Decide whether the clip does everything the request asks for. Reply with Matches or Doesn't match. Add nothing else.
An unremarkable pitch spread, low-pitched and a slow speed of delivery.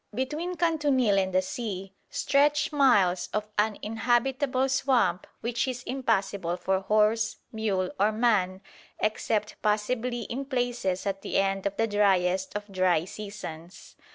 Doesn't match